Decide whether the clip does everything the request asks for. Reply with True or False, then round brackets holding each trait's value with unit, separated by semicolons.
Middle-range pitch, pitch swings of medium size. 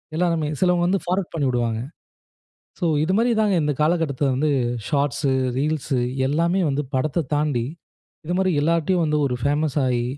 True (155 Hz; 3.6 semitones)